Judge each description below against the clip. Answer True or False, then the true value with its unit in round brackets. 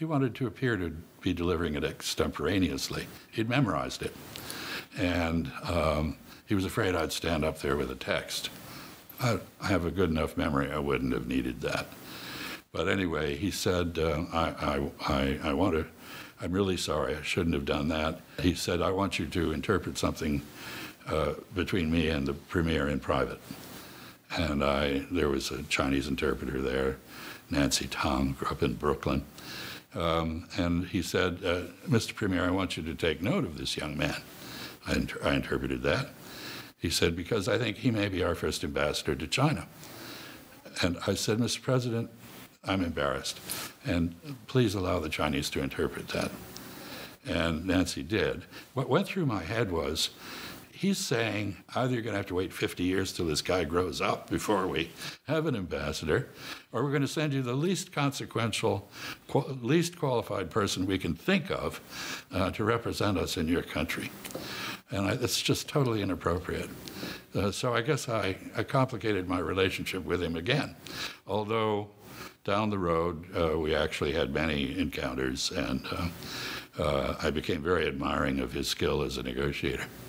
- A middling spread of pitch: False (6.4 semitones)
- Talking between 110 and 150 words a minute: False (170 wpm)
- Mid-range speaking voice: False (90 Hz)